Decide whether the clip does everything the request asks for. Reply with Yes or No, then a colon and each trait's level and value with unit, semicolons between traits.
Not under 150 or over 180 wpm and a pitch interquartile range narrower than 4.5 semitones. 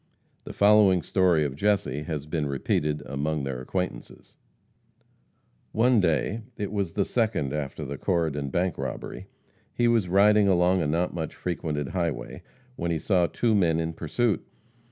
No: average, 155 wpm; average, 4.9 semitones